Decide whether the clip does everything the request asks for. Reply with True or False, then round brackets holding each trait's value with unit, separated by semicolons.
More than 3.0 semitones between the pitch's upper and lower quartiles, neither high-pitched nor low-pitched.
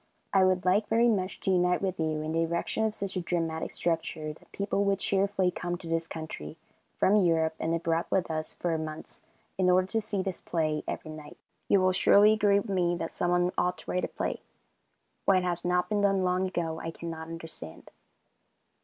False (2.7 semitones; 180 Hz)